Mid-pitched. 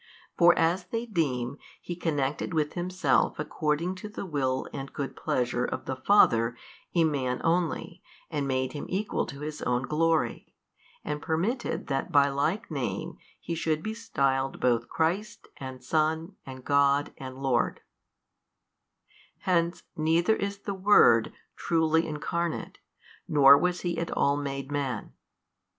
Yes: medium, 155 Hz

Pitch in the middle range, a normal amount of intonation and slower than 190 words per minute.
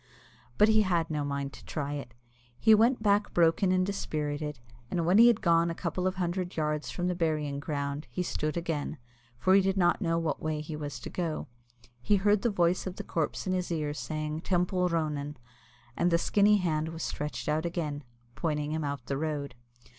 No: medium, 165 Hz; average, 3.5 semitones; fast, 205 wpm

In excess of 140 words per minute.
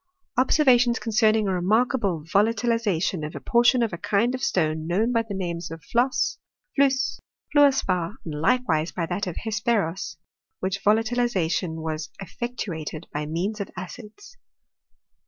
Yes: average, 150 wpm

